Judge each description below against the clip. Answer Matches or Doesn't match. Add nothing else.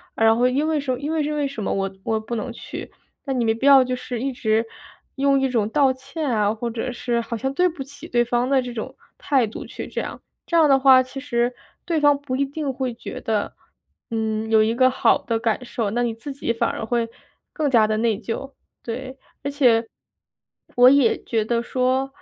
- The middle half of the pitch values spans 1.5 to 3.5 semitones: Matches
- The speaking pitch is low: Doesn't match